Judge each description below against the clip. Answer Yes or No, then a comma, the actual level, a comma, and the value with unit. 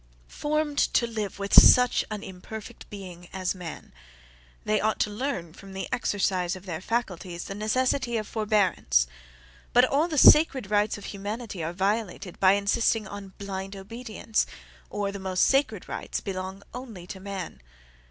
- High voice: Yes, high, 200 Hz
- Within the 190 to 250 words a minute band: No, average, 155 wpm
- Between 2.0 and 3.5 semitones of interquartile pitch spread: Yes, average, 3.2 semitones